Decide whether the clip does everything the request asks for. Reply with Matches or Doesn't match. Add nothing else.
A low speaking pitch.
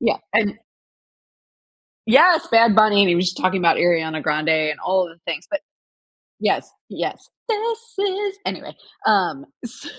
Doesn't match